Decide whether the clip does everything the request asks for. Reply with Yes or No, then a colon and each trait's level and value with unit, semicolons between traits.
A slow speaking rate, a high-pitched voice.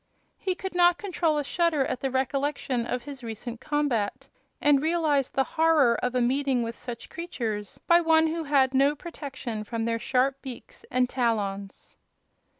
No: average, 165 wpm; very high, 270 Hz